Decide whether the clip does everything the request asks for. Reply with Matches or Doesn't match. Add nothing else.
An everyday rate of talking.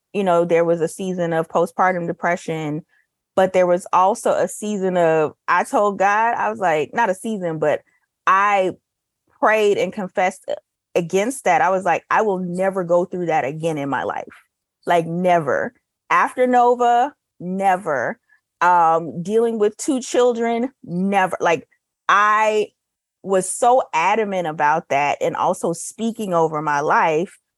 Matches